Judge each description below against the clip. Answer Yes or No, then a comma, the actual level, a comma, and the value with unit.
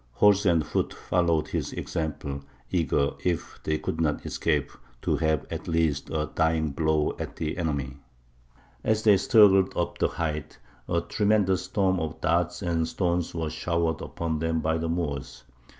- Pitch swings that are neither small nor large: No, narrow, 2.3 semitones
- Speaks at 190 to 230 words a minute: No, average, 160 wpm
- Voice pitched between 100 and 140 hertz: No, very low, 80 Hz